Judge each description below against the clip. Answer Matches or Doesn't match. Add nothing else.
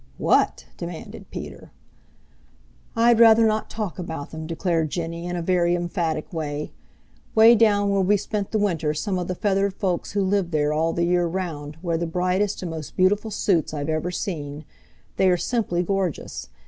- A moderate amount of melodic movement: Matches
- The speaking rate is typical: Matches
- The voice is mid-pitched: Matches